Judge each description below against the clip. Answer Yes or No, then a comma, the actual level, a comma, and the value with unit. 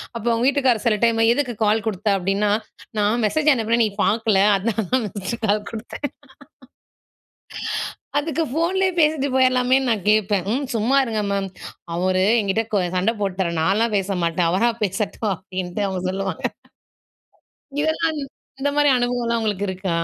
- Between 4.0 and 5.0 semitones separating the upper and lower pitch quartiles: Yes, average, 4.5 semitones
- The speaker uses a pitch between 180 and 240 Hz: Yes, high, 220 Hz